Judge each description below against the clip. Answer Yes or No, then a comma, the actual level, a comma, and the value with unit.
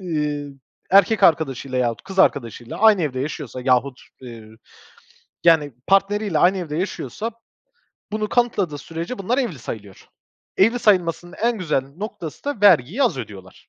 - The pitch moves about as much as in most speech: No, wide, 7.4 semitones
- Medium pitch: Yes, medium, 165 Hz